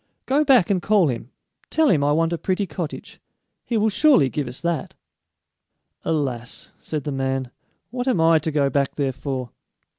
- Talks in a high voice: No, medium, 155 Hz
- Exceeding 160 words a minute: Yes, average, 180 wpm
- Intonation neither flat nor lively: No, wide, 6.5 semitones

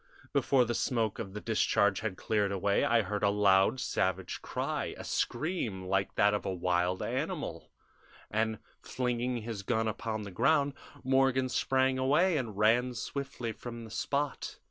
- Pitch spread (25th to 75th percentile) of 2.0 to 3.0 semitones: No, average, 4.2 semitones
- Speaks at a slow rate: No, average, 160 wpm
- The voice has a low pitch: Yes, low, 110 Hz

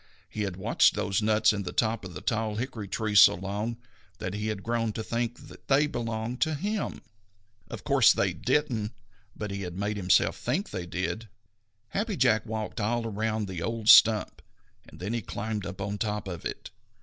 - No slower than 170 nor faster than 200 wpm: Yes, average, 195 wpm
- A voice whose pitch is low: Yes, low, 110 Hz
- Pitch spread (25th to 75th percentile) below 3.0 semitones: Yes, narrow, 2.5 semitones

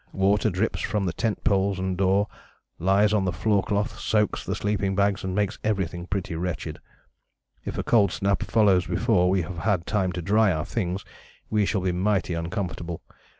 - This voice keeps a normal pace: Yes, average, 185 wpm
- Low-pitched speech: Yes, very low, 95 Hz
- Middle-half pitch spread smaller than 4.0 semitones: Yes, narrow, 2.4 semitones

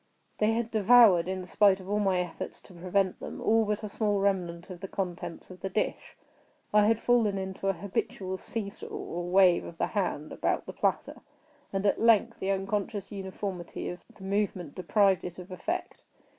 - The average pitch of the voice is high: Yes, high, 195 Hz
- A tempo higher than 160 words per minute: Yes, average, 190 wpm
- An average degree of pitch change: No, narrow, 2.2 semitones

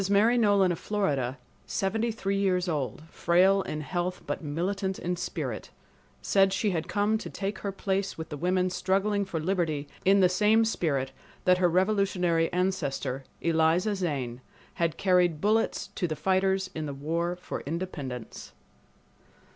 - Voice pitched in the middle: Yes, medium, 180 Hz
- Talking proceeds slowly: No, average, 155 wpm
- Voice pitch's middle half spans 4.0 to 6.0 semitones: No, average, 3.4 semitones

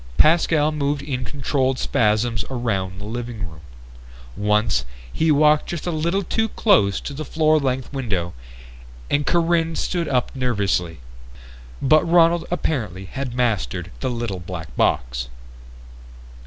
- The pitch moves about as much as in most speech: No, wide, 7.0 semitones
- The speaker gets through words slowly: Yes, slow, 130 wpm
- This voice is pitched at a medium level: No, low, 130 Hz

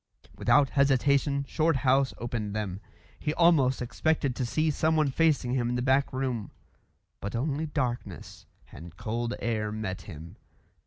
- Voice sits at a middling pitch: No, low, 130 Hz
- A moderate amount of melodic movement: Yes, average, 3.6 semitones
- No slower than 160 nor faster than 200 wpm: No, average, 140 wpm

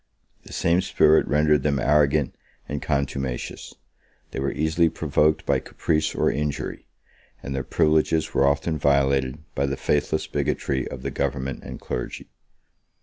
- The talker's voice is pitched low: Yes, very low, 70 Hz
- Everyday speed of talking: Yes, average, 145 wpm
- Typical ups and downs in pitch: No, narrow, 2.2 semitones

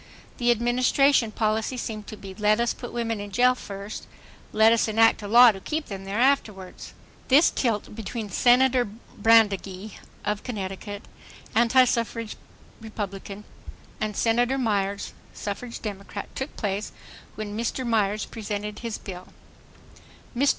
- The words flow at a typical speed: No, slow, 130 wpm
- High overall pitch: Yes, high, 220 Hz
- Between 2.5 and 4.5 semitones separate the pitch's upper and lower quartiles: Yes, average, 2.8 semitones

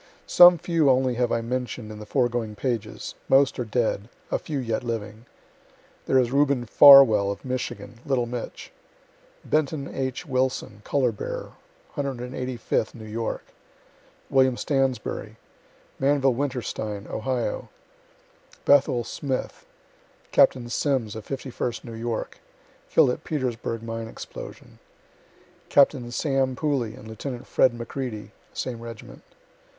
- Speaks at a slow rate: Yes, slow, 120 wpm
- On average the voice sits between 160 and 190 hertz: No, low, 125 Hz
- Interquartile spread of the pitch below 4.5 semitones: Yes, average, 2.8 semitones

